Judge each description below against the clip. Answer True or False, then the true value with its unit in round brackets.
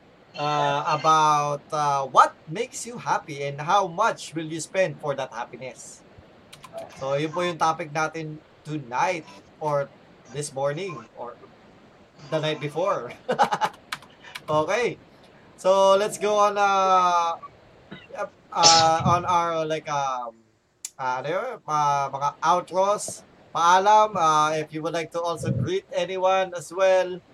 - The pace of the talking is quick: False (115 wpm)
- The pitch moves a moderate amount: True (4.0 semitones)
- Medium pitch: True (160 Hz)